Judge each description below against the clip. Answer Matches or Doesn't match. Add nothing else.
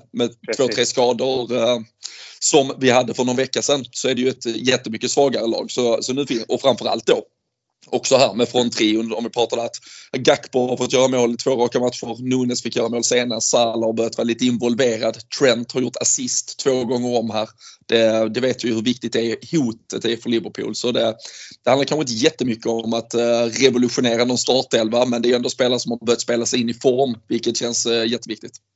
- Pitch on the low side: Matches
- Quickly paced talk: Matches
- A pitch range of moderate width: Doesn't match